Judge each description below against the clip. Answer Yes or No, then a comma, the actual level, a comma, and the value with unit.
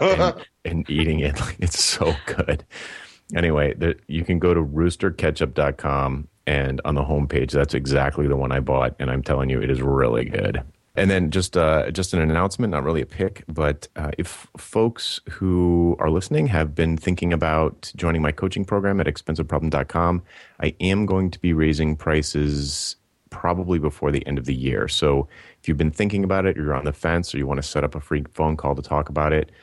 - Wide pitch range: No, average, 3.5 semitones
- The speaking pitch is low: Yes, very low, 80 Hz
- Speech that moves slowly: No, fast, 205 wpm